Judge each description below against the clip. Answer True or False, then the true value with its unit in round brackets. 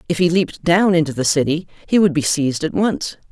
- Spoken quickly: True (235 wpm)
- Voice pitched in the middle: True (165 Hz)